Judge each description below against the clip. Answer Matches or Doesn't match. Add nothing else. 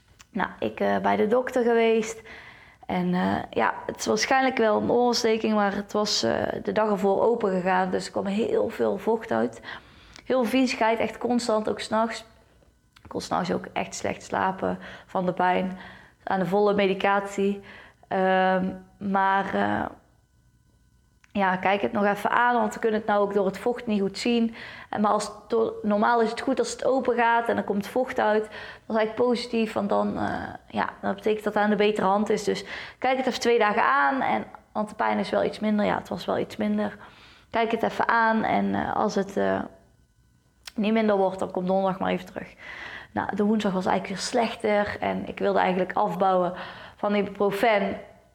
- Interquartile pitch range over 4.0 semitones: Doesn't match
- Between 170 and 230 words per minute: Matches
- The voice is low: Doesn't match